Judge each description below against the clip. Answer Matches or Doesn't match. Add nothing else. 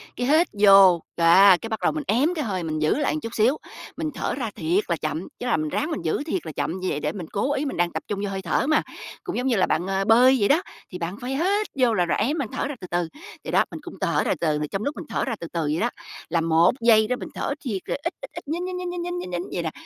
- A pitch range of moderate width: Doesn't match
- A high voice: Matches